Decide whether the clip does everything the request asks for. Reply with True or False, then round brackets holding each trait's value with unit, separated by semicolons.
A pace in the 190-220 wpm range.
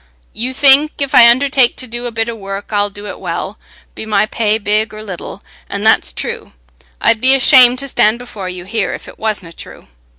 True (205 wpm)